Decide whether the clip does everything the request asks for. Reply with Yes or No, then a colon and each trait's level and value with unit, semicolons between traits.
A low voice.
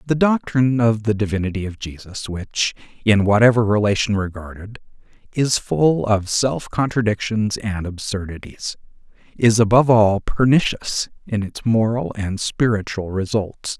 Yes: low, 110 Hz